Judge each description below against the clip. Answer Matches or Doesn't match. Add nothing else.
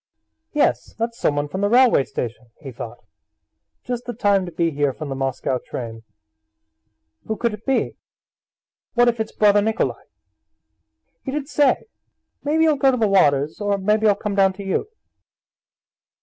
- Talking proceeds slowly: Doesn't match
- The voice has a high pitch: Matches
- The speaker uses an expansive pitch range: Matches